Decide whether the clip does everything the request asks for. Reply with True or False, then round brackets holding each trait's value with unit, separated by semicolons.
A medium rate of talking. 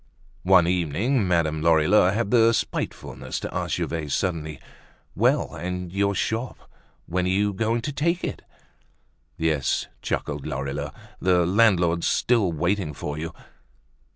False (130 wpm)